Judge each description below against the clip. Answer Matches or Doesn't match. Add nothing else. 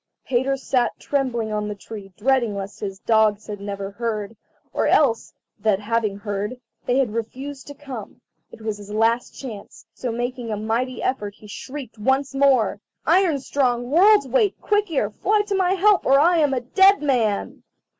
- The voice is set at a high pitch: Matches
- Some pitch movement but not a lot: Matches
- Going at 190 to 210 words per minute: Doesn't match